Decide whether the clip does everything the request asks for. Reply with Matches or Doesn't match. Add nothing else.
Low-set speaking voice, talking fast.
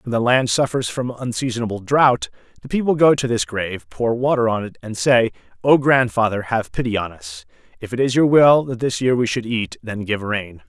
Matches